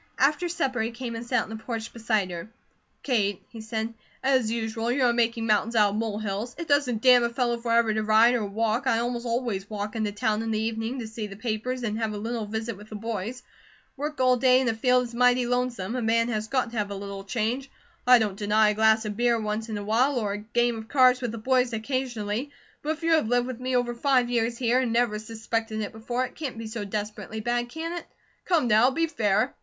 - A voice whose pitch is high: Yes, high, 230 Hz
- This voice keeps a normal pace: No, fast, 245 wpm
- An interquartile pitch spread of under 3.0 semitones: Yes, narrow, 2.5 semitones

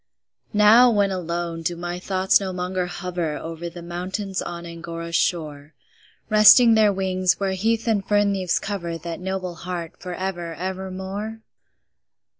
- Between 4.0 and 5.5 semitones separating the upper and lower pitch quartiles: No, narrow, 2.4 semitones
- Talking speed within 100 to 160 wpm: Yes, average, 150 wpm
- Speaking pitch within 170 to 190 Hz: Yes, medium, 185 Hz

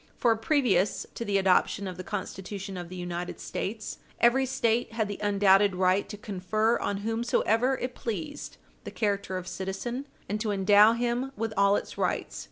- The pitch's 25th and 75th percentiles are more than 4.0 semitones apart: No, average, 3.3 semitones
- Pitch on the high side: Yes, high, 205 Hz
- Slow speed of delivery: No, average, 175 wpm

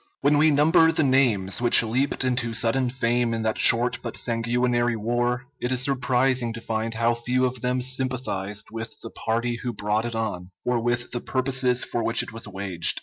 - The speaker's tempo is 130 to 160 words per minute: No, average, 200 wpm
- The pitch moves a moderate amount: No, narrow, 2.0 semitones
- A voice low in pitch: Yes, low, 120 Hz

